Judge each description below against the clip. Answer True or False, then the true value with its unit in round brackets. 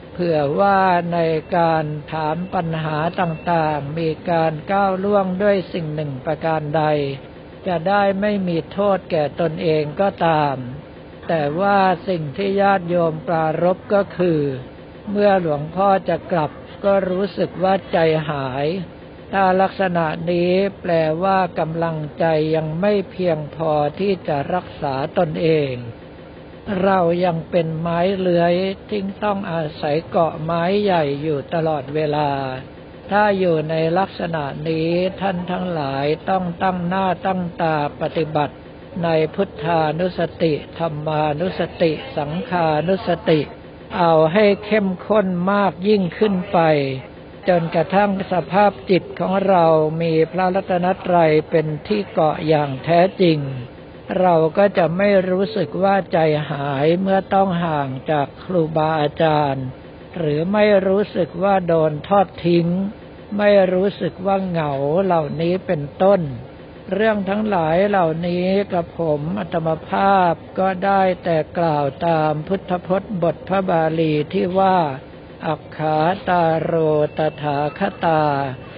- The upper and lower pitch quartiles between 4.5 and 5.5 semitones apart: False (3.5 semitones)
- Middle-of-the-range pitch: True (170 Hz)